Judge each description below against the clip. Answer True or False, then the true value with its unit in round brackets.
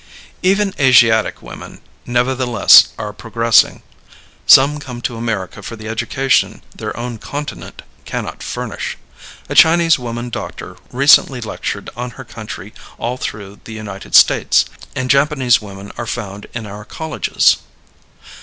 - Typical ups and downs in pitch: True (3.5 semitones)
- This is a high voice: False (120 Hz)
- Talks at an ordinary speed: False (130 wpm)